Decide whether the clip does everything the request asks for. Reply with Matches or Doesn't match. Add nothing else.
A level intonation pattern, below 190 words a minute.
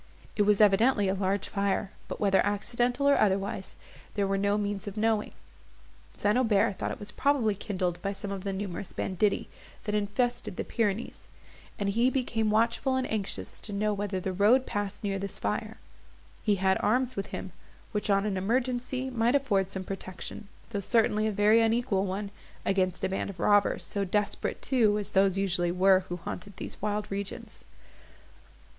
Matches